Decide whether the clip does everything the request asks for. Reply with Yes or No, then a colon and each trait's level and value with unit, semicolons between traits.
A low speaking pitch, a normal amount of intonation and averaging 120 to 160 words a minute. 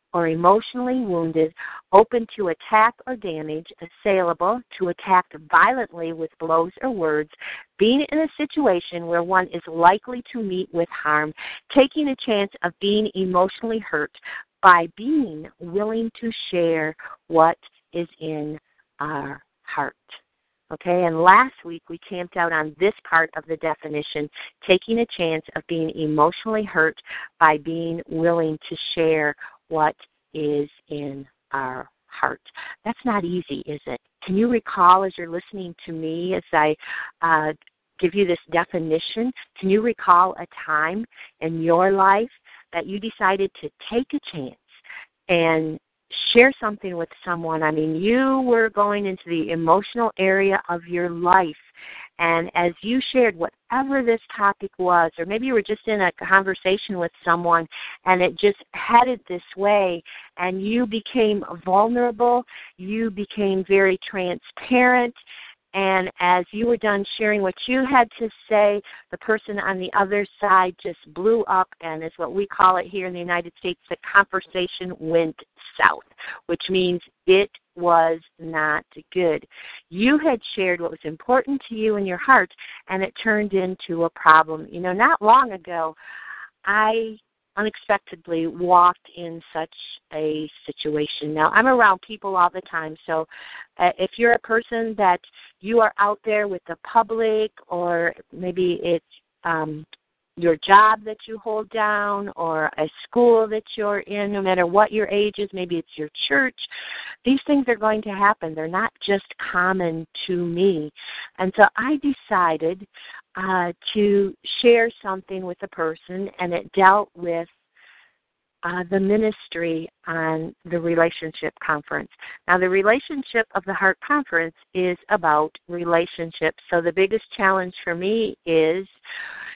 No: medium, 185 Hz; average, 4.2 semitones; average, 150 wpm